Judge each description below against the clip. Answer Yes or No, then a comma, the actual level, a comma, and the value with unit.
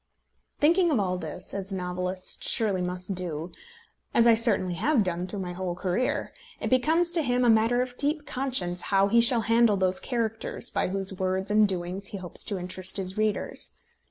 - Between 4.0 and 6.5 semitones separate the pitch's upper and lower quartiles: Yes, average, 4.5 semitones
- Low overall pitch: No, high, 195 Hz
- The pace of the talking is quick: No, average, 190 wpm